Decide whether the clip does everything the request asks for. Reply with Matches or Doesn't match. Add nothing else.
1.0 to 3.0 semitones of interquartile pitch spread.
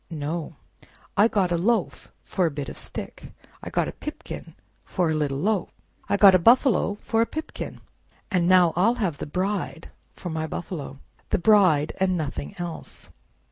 Doesn't match